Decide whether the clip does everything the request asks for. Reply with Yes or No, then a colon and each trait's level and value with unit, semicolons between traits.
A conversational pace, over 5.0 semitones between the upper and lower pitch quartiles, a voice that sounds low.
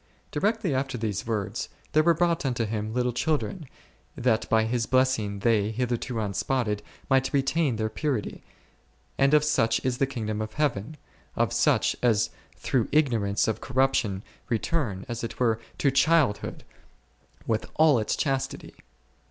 No: average, 145 wpm; average, 4.2 semitones; low, 125 Hz